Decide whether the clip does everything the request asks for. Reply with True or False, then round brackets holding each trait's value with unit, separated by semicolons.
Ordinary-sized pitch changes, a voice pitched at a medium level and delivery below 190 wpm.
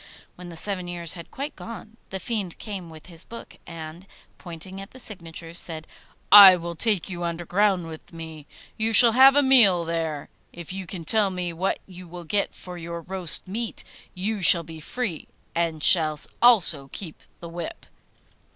True (3.4 semitones; 175 Hz; 180 wpm)